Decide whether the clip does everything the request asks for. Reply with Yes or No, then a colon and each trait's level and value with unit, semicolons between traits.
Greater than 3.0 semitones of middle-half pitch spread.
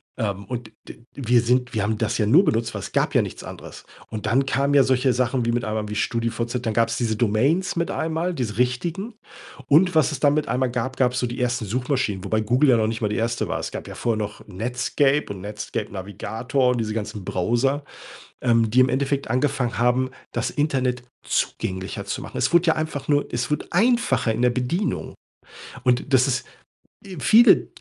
Yes: average, 3.7 semitones